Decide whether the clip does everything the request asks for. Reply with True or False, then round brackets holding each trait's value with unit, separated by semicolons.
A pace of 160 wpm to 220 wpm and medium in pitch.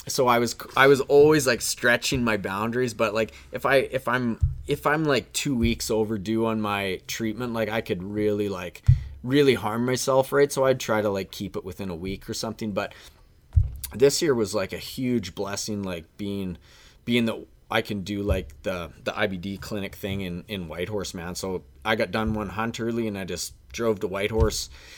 False (200 wpm; 105 Hz)